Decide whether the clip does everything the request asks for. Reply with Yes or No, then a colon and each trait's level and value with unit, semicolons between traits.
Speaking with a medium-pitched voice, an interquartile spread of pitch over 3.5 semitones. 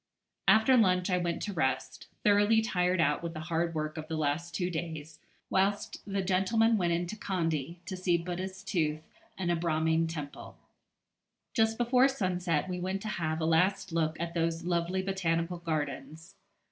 No: medium, 175 Hz; average, 2.8 semitones